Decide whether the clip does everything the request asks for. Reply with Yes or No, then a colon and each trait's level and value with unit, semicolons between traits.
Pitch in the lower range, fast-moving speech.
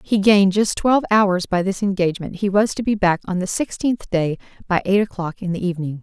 No: high, 195 Hz; fast, 230 wpm